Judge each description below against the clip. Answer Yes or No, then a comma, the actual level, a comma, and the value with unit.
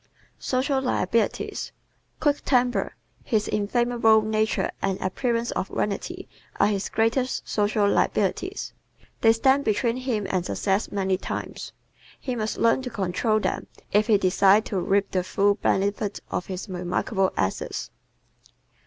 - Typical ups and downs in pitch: Yes, average, 3.5 semitones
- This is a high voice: Yes, high, 215 Hz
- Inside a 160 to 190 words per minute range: No, slow, 135 wpm